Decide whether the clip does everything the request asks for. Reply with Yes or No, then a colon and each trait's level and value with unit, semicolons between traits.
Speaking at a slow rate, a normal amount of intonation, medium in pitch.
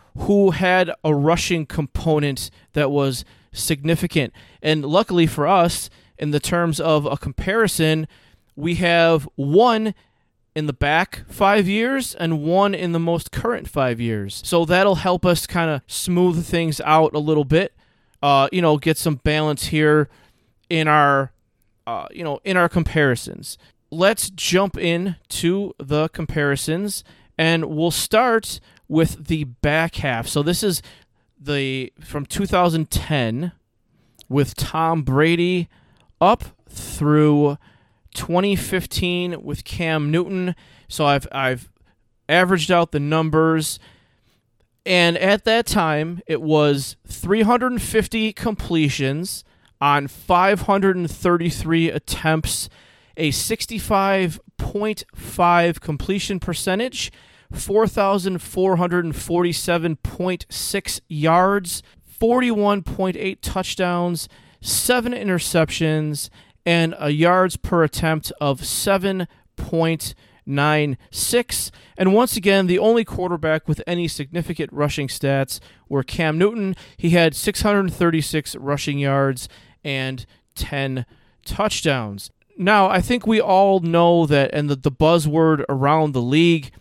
Yes: slow, 110 wpm; average, 4.3 semitones; medium, 160 Hz